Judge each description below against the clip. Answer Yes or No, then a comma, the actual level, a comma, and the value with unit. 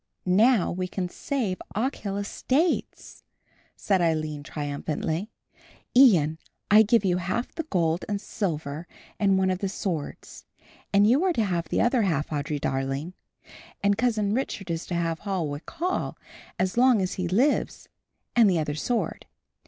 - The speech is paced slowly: No, average, 155 wpm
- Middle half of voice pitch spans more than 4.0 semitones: Yes, average, 5.2 semitones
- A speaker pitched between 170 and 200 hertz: Yes, high, 190 Hz